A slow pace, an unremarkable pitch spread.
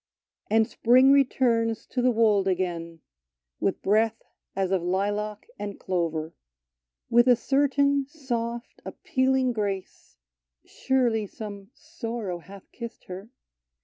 Yes: slow, 115 wpm; average, 4.5 semitones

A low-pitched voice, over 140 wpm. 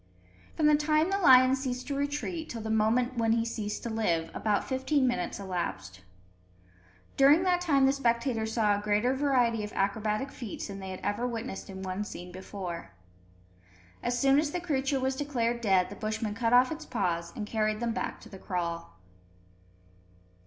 No: high, 230 Hz; average, 180 wpm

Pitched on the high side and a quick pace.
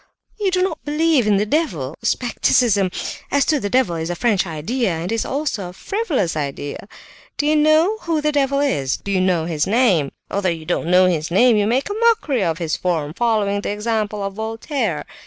Yes: high, 210 Hz; fast, 210 wpm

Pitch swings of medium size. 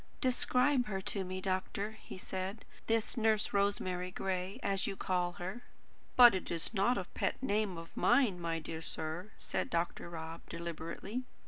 Yes: average, 3.6 semitones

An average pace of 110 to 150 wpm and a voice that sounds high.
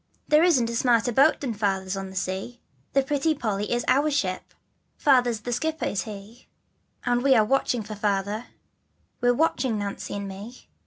No: average, 175 wpm; high, 235 Hz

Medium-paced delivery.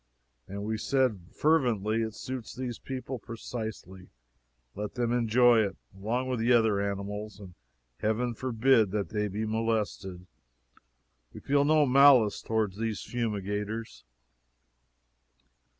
No: slow, 120 wpm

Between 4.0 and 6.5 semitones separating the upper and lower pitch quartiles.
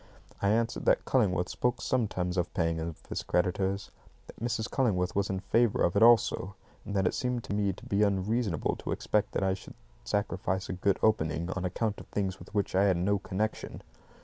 No: average, 2.8 semitones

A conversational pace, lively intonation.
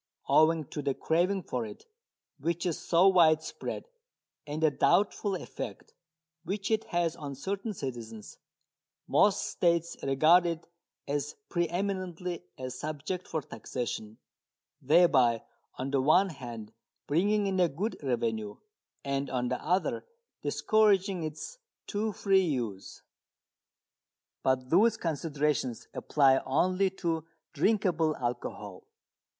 No: slow, 120 wpm; wide, 5.7 semitones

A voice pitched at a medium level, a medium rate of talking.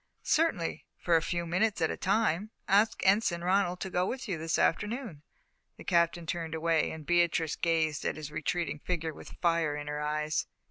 Yes: medium, 170 Hz; average, 185 wpm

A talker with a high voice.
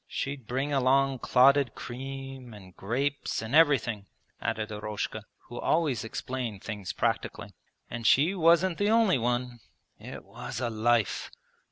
No: low, 125 Hz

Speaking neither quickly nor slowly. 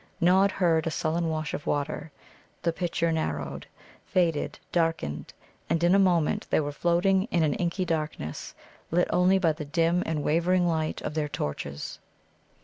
Yes: average, 160 wpm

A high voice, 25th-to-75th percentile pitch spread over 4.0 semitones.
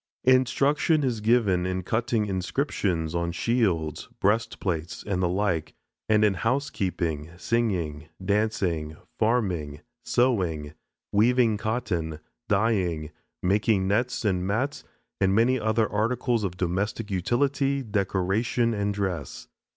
No: low, 105 Hz; average, 4.6 semitones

